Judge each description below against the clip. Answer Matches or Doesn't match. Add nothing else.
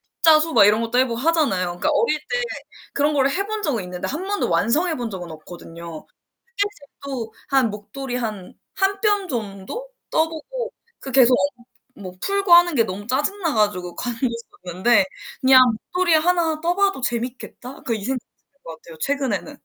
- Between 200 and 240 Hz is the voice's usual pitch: Doesn't match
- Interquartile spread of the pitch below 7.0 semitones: Doesn't match